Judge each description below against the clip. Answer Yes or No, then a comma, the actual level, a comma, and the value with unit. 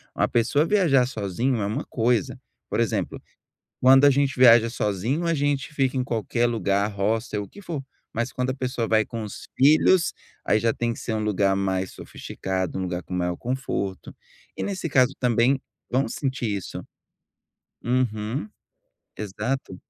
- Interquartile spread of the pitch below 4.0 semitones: No, average, 4.3 semitones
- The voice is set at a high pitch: No, low, 120 Hz